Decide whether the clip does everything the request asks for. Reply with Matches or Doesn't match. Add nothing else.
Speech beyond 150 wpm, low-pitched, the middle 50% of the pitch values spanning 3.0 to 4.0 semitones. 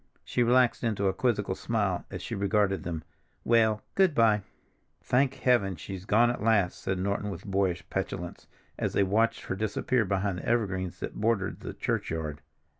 Matches